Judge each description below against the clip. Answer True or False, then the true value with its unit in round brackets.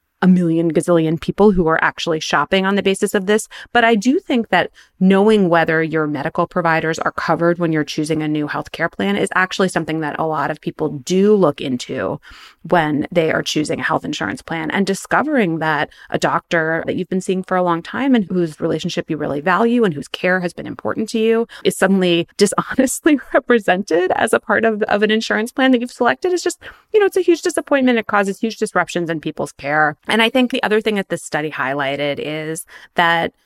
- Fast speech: True (215 wpm)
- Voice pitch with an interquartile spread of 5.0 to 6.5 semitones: True (5.4 semitones)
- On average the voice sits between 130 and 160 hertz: False (180 Hz)